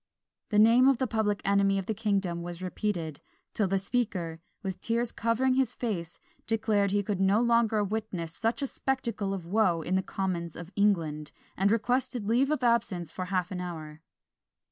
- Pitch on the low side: No, high, 200 Hz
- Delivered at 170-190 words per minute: Yes, average, 180 wpm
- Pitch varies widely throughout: No, average, 4.2 semitones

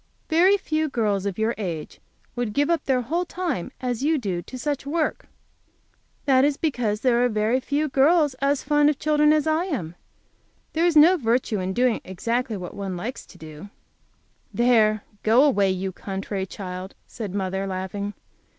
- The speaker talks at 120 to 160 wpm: No, average, 175 wpm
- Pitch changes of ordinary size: No, wide, 6.9 semitones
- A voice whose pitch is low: No, high, 245 Hz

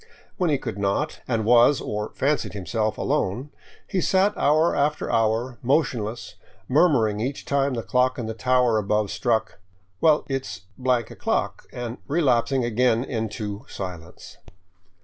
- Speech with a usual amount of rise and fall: Yes, average, 4.2 semitones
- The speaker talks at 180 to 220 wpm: No, average, 145 wpm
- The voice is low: Yes, low, 120 Hz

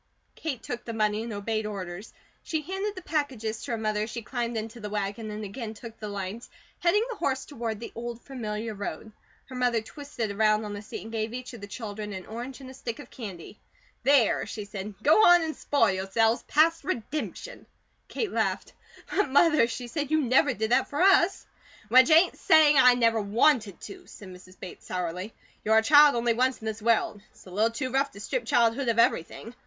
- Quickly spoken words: Yes, fast, 210 wpm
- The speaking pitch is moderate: No, high, 230 Hz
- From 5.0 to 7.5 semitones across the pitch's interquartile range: No, average, 4.3 semitones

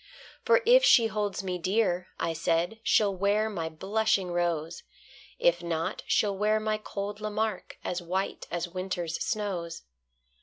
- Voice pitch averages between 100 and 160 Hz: No, high, 190 Hz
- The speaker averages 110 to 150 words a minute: Yes, average, 145 wpm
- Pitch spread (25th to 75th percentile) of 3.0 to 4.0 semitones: Yes, average, 3.6 semitones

